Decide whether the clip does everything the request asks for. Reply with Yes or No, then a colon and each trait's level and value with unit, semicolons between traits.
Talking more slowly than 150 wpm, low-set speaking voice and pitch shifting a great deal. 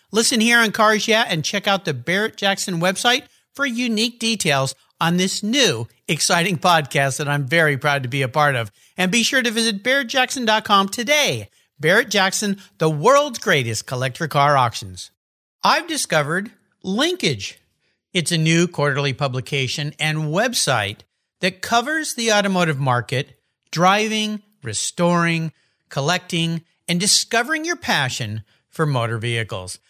No: average, 140 wpm; medium, 180 Hz; wide, 7.3 semitones